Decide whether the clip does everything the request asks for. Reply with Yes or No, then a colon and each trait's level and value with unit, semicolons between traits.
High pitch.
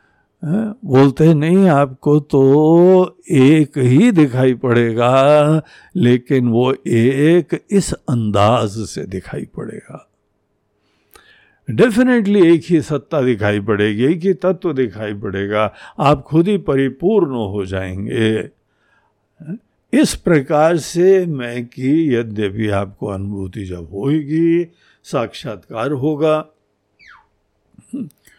No: low, 135 Hz